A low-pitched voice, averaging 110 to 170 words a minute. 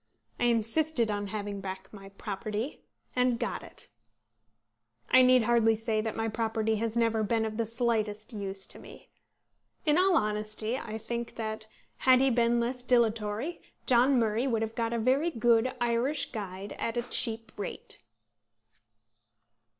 No: high, 225 Hz; average, 155 wpm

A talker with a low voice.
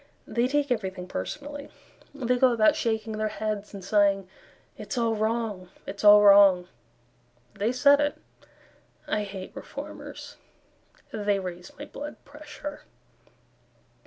No: high, 215 Hz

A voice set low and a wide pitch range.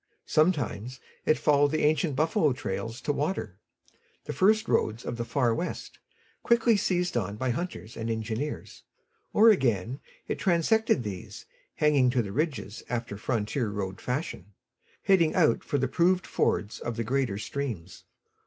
Yes: low, 130 Hz; wide, 6.0 semitones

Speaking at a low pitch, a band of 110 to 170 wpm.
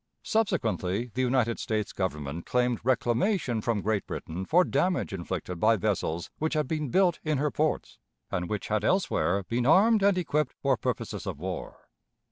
Yes: low, 120 Hz; average, 165 wpm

